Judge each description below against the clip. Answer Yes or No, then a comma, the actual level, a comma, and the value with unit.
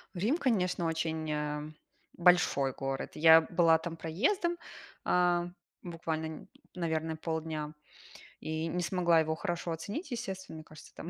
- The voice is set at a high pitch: No, medium, 165 Hz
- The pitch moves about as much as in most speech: No, narrow, 2.1 semitones